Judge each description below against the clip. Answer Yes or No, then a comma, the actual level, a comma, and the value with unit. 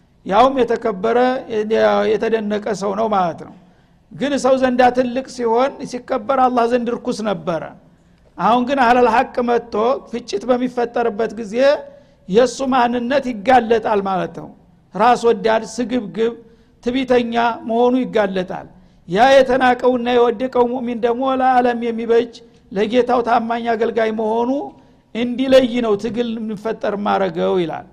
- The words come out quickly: Yes, fast, 115 wpm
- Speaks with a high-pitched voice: Yes, high, 235 Hz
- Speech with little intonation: Yes, narrow, 2.3 semitones